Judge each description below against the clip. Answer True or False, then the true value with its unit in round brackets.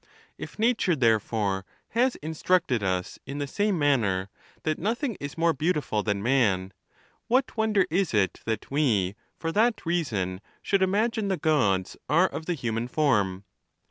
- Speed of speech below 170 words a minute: True (150 wpm)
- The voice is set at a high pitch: False (145 Hz)